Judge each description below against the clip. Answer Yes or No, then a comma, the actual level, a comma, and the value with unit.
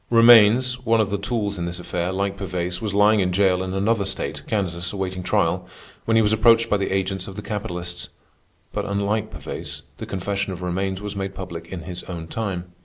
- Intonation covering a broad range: No, narrow, 2.5 semitones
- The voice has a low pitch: Yes, very low, 95 Hz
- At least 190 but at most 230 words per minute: Yes, fast, 205 wpm